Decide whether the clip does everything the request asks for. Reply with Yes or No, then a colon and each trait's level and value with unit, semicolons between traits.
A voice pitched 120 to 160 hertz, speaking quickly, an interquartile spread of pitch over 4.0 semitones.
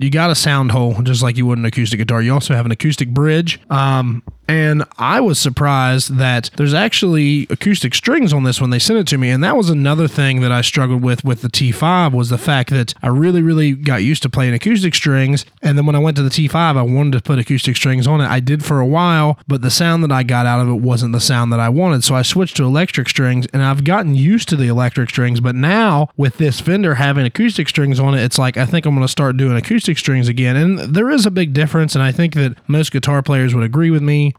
No: medium, 140 Hz; fast, 260 wpm; average, 3.6 semitones